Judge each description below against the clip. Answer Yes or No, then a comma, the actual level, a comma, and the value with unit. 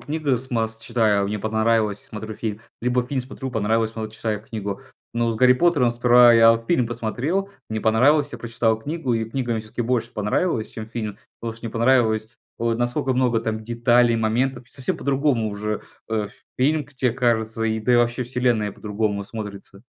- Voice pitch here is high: No, low, 115 Hz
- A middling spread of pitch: No, narrow, 2.2 semitones